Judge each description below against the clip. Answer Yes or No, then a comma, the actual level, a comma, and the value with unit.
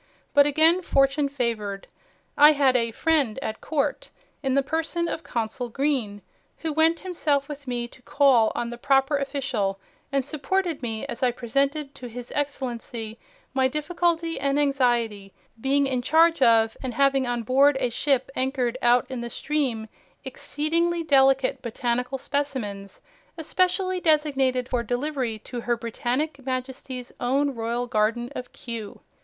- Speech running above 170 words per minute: No, average, 150 wpm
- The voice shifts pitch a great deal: No, average, 3.4 semitones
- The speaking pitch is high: Yes, very high, 265 Hz